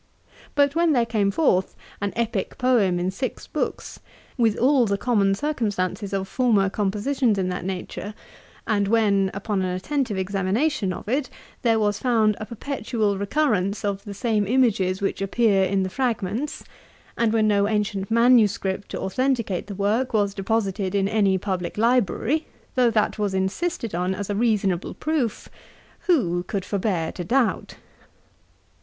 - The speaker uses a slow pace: No, average, 155 wpm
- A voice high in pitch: Yes, high, 210 Hz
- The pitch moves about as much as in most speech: Yes, average, 3.6 semitones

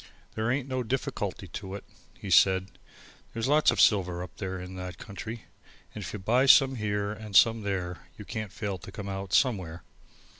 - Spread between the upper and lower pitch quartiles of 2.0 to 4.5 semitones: Yes, average, 3.4 semitones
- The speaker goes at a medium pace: Yes, average, 190 wpm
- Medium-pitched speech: No, low, 100 Hz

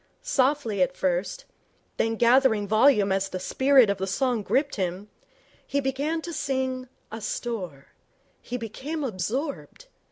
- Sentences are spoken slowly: Yes, slow, 130 wpm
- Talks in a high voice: Yes, high, 245 Hz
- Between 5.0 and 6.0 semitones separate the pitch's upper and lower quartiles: Yes, wide, 5.4 semitones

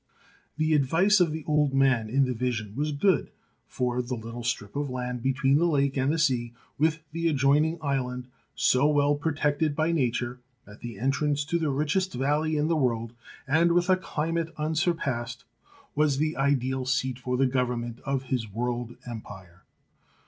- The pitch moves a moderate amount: Yes, average, 3.6 semitones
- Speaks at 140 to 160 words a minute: No, average, 175 wpm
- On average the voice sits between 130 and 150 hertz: Yes, low, 135 Hz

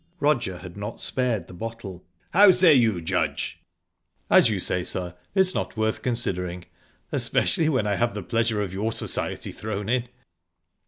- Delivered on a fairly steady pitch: No, average, 4.8 semitones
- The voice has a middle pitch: No, low, 110 Hz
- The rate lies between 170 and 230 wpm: No, average, 160 wpm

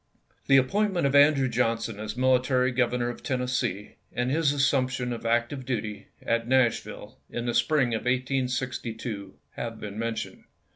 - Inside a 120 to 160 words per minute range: No, average, 175 wpm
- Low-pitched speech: Yes, low, 125 Hz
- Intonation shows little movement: Yes, narrow, 2.2 semitones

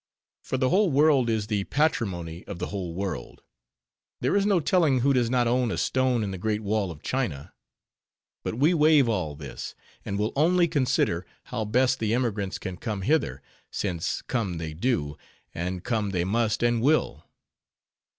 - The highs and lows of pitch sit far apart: Yes, wide, 5.7 semitones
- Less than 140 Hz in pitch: Yes, low, 115 Hz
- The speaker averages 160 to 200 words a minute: Yes, average, 175 wpm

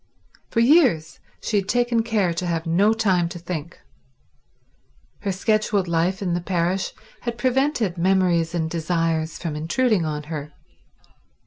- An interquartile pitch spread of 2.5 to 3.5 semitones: No, average, 4.5 semitones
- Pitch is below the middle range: No, medium, 180 Hz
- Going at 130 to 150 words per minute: Yes, average, 140 wpm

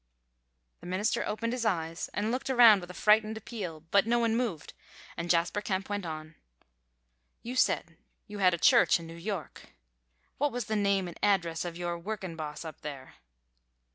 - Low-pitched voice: No, high, 195 Hz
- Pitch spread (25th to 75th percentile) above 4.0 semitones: Yes, average, 4.5 semitones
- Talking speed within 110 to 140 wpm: No, average, 180 wpm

